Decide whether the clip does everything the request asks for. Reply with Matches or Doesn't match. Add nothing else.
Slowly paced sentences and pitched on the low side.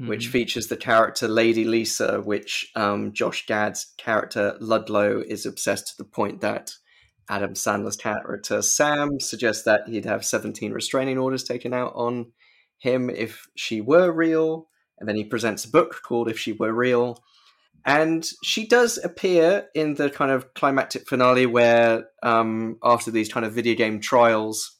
Doesn't match